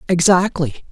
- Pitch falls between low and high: Yes, medium, 175 Hz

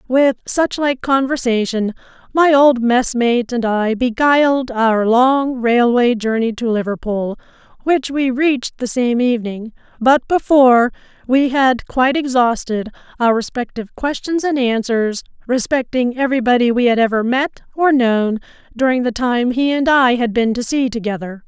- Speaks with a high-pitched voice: Yes, high, 245 Hz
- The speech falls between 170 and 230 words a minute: No, average, 145 wpm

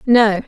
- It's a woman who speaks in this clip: Yes, female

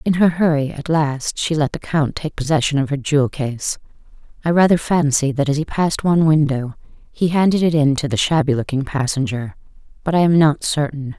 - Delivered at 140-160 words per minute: No, fast, 205 wpm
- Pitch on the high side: No, medium, 150 Hz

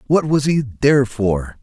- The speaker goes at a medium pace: Yes, average, 185 wpm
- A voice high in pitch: No, low, 125 Hz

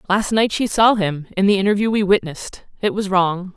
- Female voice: Yes, female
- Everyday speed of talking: No, fast, 220 wpm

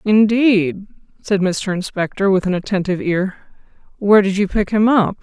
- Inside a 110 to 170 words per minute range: Yes, average, 160 wpm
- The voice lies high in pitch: Yes, high, 200 Hz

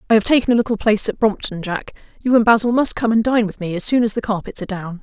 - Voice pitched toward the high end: Yes, high, 215 Hz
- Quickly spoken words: Yes, fast, 285 wpm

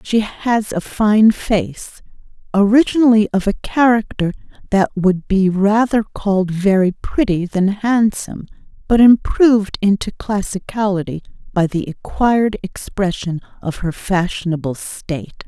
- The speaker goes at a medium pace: No, slow, 110 wpm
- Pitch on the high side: Yes, high, 200 Hz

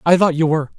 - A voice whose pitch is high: No, medium, 160 Hz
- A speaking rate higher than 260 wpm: Yes, fast, 305 wpm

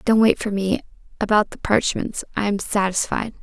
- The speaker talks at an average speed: Yes, average, 175 wpm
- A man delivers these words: No, female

